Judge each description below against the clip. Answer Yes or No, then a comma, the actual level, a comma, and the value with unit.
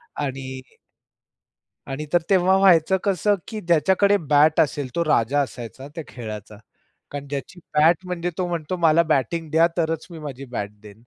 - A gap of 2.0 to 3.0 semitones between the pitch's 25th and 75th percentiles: No, average, 4.4 semitones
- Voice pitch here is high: No, medium, 155 Hz